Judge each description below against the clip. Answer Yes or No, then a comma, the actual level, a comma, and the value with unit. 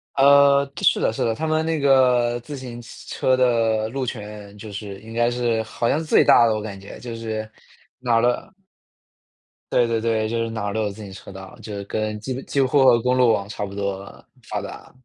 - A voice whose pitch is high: No, low, 115 Hz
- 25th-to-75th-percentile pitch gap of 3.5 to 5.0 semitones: No, average, 3.0 semitones